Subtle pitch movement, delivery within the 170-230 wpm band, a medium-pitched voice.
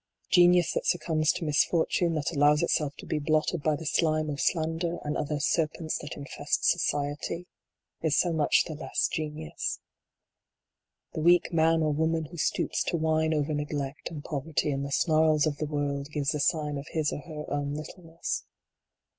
Yes: narrow, 1.9 semitones; average, 175 wpm; medium, 155 Hz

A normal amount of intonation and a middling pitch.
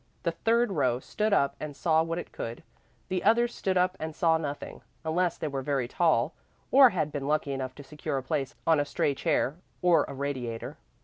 Yes: average, 4.3 semitones; medium, 155 Hz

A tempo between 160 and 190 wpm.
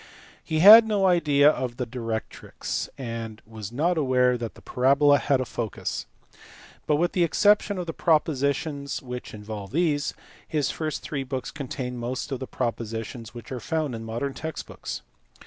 Yes: average, 170 wpm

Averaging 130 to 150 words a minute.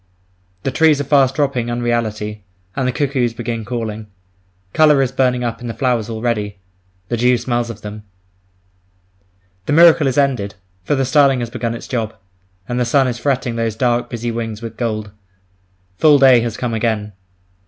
No: average, 175 wpm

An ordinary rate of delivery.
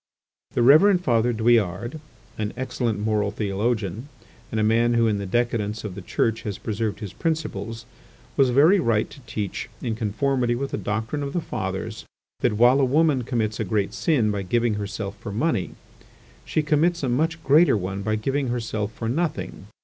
Yes: average, 180 wpm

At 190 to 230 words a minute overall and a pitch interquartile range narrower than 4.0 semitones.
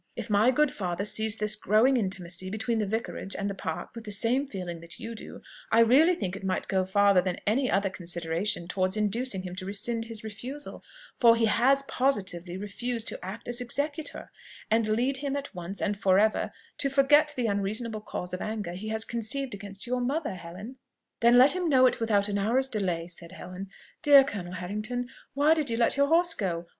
No: fast, 205 wpm; average, 4.7 semitones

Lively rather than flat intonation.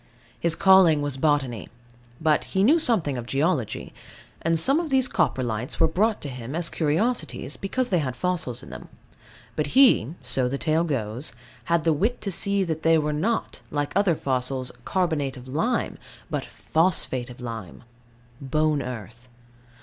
Yes: wide, 6.0 semitones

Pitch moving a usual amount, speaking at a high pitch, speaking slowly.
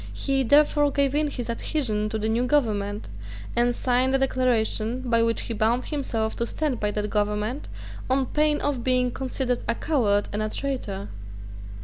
No: average, 3.6 semitones; high, 245 Hz; average, 170 wpm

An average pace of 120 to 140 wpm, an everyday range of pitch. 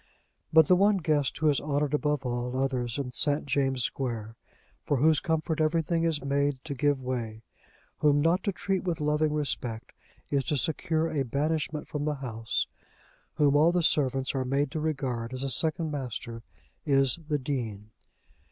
No: average, 170 wpm; average, 3.2 semitones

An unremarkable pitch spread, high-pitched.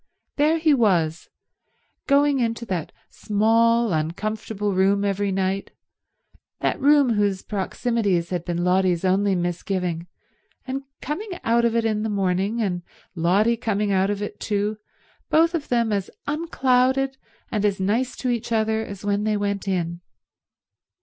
Yes: average, 3.8 semitones; high, 210 Hz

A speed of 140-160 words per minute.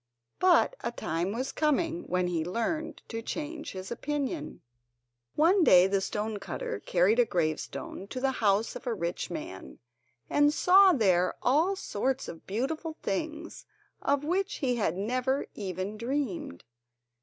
Yes: average, 145 wpm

